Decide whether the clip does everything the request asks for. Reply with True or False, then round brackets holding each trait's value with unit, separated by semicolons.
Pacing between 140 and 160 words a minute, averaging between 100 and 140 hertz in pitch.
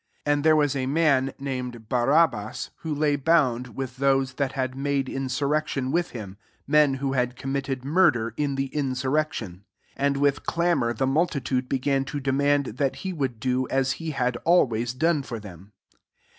False (185 wpm; 135 Hz)